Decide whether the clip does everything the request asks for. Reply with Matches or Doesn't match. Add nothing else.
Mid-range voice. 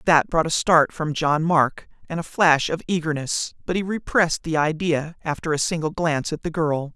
Matches